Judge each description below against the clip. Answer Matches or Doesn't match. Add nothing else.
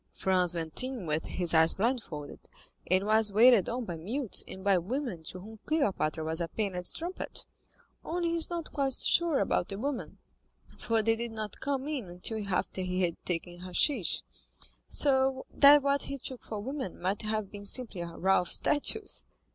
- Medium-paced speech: Matches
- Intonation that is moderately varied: Doesn't match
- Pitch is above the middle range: Matches